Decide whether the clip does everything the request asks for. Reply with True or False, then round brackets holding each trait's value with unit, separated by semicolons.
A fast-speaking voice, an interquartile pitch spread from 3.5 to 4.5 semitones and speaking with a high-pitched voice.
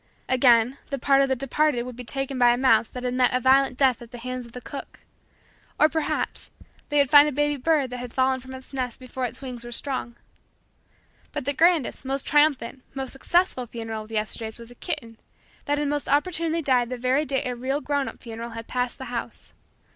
False (225 wpm; 2.6 semitones; 260 Hz)